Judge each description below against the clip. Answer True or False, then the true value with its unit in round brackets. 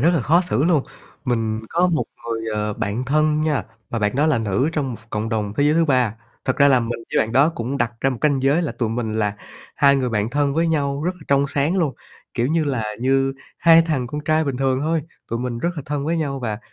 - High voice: False (135 Hz)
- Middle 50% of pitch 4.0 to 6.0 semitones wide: True (4.6 semitones)